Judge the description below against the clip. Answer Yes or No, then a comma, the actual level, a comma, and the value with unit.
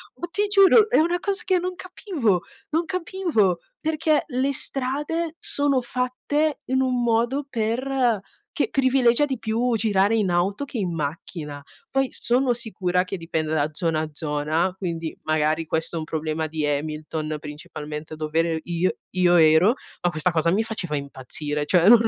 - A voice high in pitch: Yes, high, 200 Hz